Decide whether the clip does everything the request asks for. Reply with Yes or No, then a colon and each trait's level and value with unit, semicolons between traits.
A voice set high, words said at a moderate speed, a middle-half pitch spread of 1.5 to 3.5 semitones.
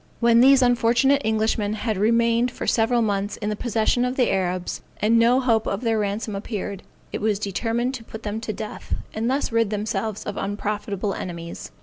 Yes: high, 220 Hz; average, 190 wpm; narrow, 2.4 semitones